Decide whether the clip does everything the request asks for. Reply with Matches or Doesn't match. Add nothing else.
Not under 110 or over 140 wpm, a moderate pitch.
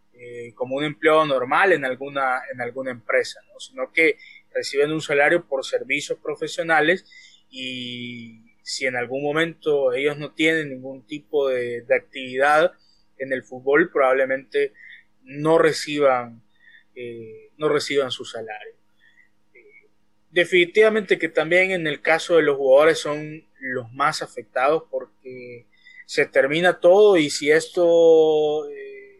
Matches